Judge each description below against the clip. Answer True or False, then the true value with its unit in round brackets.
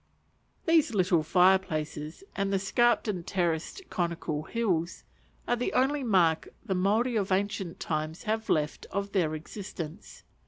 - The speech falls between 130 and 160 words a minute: True (145 wpm)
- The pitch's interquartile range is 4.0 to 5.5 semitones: True (4.9 semitones)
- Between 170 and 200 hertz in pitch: True (190 Hz)